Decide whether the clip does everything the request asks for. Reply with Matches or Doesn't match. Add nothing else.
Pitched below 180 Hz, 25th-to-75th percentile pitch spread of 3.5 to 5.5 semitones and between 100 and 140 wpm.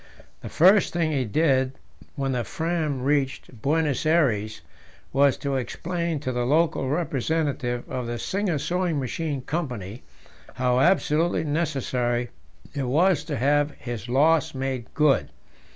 Matches